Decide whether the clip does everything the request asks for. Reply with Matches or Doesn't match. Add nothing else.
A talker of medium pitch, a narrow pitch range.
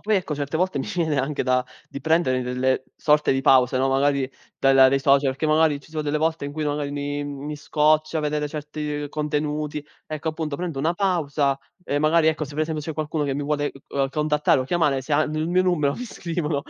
Matches